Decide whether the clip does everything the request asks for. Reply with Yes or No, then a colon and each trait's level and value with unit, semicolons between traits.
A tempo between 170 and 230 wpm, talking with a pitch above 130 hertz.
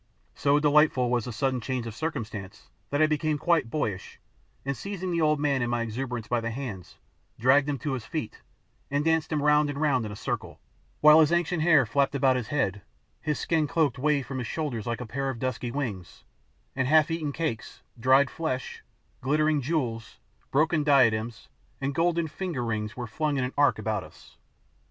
Yes: average, 195 wpm; medium, 140 Hz